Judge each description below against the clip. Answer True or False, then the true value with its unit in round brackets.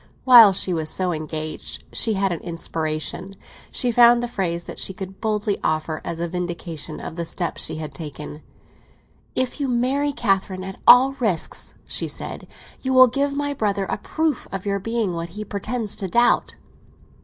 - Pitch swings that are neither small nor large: False (6.1 semitones)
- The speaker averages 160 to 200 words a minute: True (180 wpm)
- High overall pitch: True (195 Hz)